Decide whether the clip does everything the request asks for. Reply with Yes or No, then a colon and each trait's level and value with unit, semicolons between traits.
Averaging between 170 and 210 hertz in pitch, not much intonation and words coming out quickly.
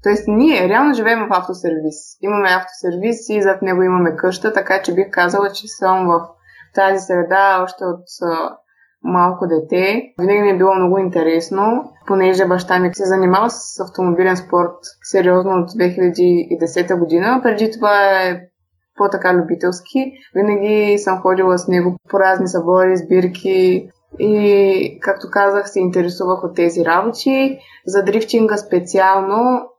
No: high, 190 Hz; narrow, 2.2 semitones; average, 145 wpm